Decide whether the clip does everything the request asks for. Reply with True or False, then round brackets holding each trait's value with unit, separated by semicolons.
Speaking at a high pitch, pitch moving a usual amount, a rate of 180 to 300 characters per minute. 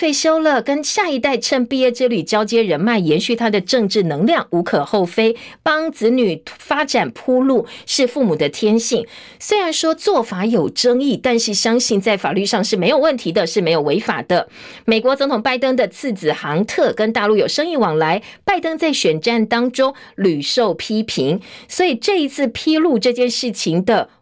True (240 Hz; 4.3 semitones; 275 characters per minute)